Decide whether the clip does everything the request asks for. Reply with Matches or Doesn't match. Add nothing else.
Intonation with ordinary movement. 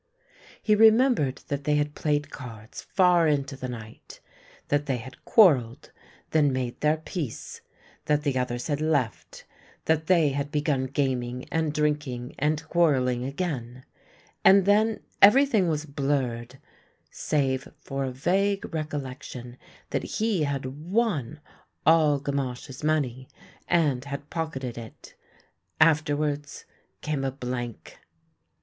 Matches